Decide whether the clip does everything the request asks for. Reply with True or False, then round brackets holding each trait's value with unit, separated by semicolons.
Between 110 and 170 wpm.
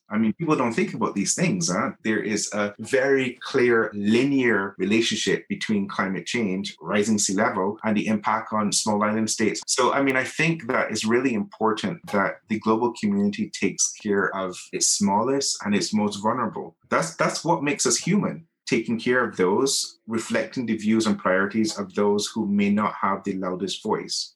False (185 wpm)